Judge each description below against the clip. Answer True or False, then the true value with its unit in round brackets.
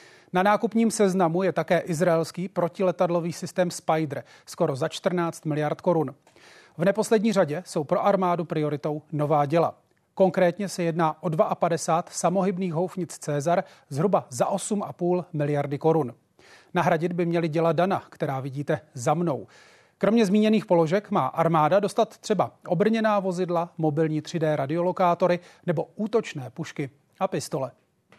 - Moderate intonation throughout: True (3.1 semitones)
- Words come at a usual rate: True (130 wpm)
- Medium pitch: True (175 Hz)